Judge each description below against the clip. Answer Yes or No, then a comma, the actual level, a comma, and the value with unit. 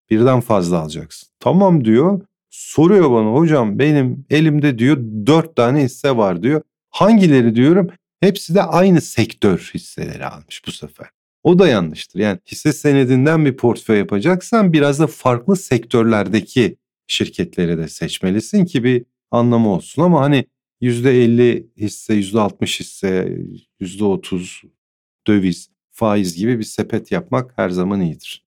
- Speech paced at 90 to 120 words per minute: No, average, 135 wpm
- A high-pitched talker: No, low, 125 Hz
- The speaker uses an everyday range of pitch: No, wide, 6.3 semitones